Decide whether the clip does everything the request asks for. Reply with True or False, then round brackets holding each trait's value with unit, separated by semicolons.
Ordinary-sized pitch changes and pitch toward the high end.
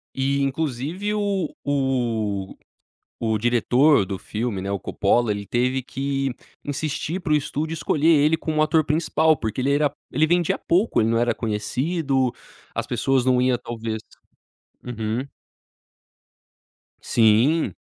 False (4.8 semitones; 135 Hz)